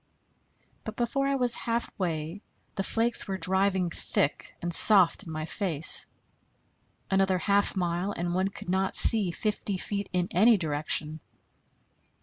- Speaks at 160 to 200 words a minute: No, slow, 135 wpm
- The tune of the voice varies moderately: Yes, average, 3.2 semitones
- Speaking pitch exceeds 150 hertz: Yes, high, 190 Hz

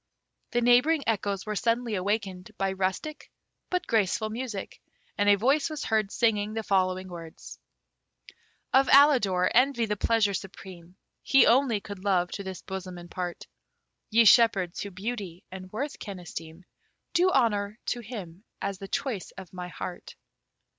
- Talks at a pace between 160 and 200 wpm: No, average, 150 wpm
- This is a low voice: No, high, 205 Hz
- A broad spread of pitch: No, average, 4.0 semitones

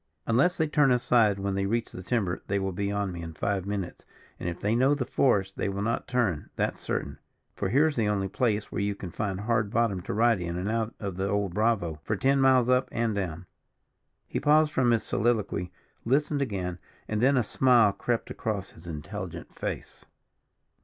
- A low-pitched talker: Yes, low, 105 Hz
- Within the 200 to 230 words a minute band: Yes, fast, 205 wpm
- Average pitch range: Yes, average, 3.9 semitones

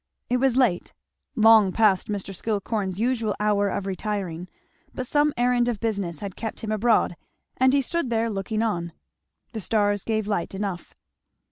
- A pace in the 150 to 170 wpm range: Yes, average, 160 wpm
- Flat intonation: No, average, 3.1 semitones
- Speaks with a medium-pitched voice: No, high, 215 Hz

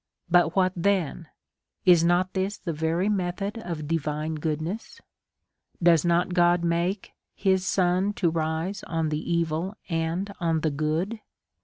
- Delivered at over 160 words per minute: No, average, 140 wpm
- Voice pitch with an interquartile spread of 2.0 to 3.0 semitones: Yes, narrow, 2.6 semitones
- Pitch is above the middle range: No, medium, 175 Hz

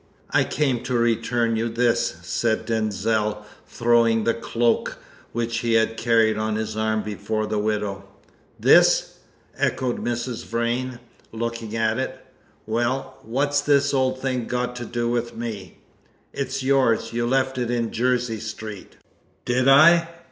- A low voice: Yes, low, 115 Hz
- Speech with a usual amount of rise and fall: No, narrow, 2.1 semitones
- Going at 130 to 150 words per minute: Yes, average, 140 wpm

